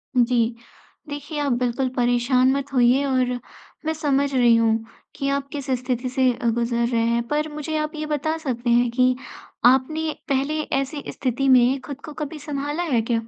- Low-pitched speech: No, very high, 265 Hz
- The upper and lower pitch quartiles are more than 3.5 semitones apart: No, average, 3.2 semitones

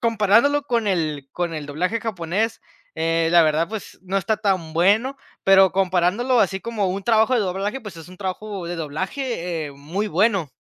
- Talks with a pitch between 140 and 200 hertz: Yes, high, 190 Hz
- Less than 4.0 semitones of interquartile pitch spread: No, average, 4.5 semitones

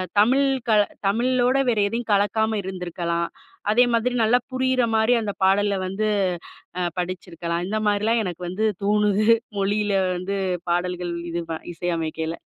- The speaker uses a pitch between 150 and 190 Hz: No, high, 205 Hz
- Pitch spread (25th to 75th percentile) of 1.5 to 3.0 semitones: No, average, 3.7 semitones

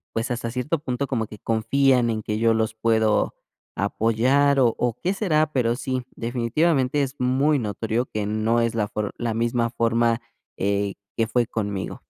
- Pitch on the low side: Yes, low, 115 Hz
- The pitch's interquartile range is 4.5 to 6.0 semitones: No, average, 2.7 semitones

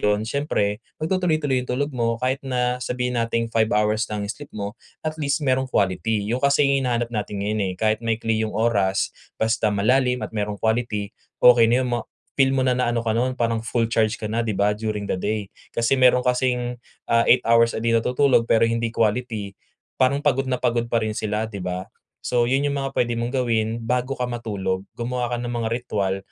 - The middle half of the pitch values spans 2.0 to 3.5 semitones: Yes, narrow, 2.6 semitones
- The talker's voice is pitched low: Yes, low, 115 Hz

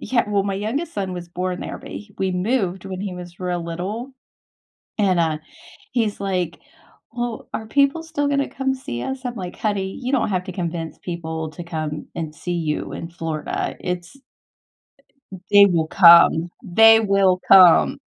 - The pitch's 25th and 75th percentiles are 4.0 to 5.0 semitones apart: Yes, average, 4.3 semitones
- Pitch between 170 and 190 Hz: Yes, medium, 185 Hz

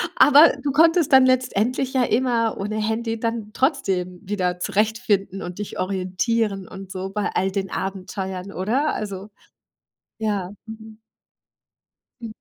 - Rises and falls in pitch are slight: No, average, 3.5 semitones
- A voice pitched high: Yes, high, 210 Hz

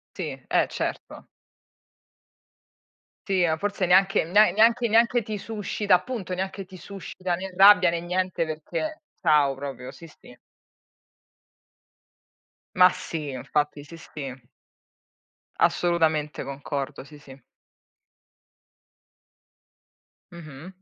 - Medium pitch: Yes, medium, 175 Hz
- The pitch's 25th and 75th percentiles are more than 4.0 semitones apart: Yes, average, 4.7 semitones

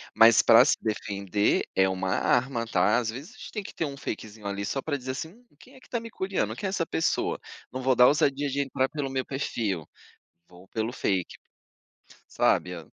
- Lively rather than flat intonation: Yes, wide, 6.0 semitones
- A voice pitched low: Yes, low, 130 Hz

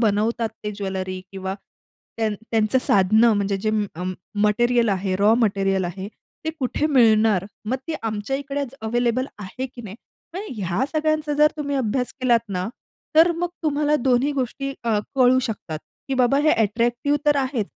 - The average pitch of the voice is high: Yes, high, 230 Hz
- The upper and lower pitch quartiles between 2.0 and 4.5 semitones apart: No, average, 4.9 semitones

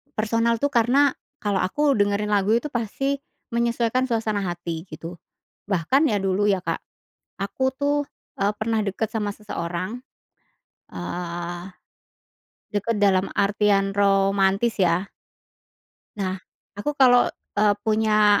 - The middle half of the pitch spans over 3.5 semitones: No, average, 3.1 semitones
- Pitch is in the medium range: No, high, 205 Hz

